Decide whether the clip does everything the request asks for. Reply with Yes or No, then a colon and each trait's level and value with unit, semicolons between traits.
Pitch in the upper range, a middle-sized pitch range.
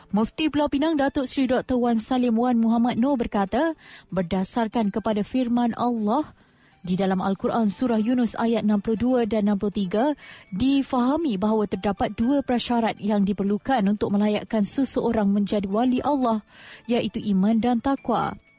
Yes: high, 230 Hz; average, 3.2 semitones